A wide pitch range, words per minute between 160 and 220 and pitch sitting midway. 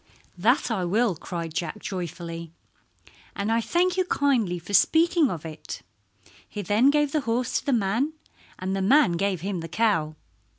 No: wide, 7.1 semitones; average, 170 wpm; high, 205 Hz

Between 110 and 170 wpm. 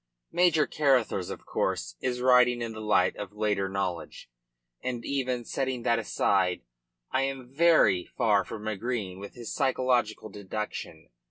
Yes: average, 145 wpm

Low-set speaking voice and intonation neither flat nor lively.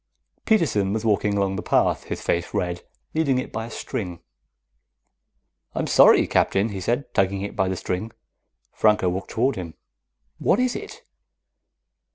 Yes: low, 100 Hz; average, 4.4 semitones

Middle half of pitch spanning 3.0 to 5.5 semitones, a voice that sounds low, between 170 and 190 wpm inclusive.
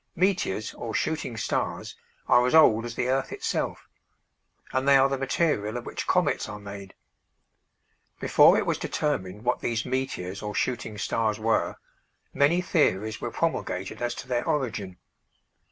No: average, 4.3 semitones; low, 120 Hz; average, 155 wpm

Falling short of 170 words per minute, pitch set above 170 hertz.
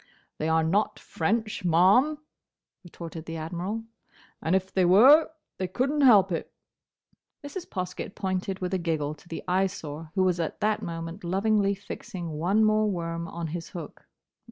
Yes: average, 155 wpm; medium, 185 Hz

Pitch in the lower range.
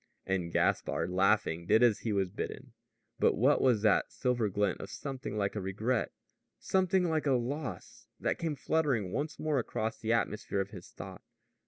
Yes: low, 115 Hz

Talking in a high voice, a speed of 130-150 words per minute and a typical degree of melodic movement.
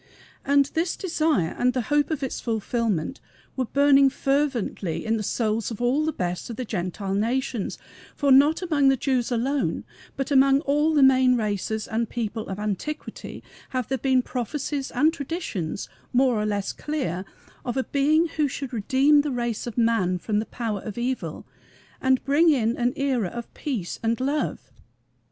No: very high, 255 Hz; average, 175 wpm; average, 4.2 semitones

